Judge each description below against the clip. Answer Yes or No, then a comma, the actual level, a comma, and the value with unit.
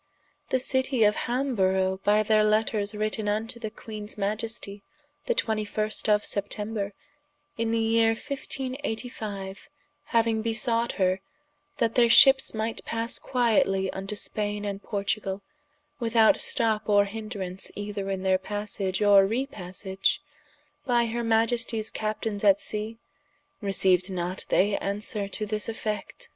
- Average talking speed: No, slow, 125 wpm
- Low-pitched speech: No, high, 215 Hz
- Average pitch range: No, narrow, 2.3 semitones